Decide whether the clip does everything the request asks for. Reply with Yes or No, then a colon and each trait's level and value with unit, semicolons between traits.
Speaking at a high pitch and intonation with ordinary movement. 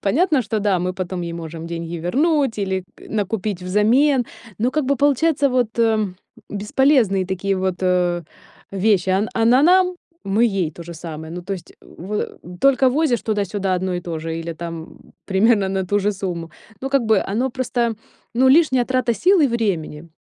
No: high, 205 Hz; wide, 5.8 semitones